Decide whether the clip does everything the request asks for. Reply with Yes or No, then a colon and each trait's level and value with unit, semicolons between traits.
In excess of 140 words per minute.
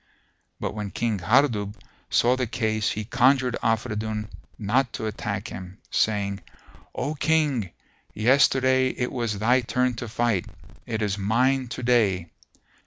No: slow, 135 wpm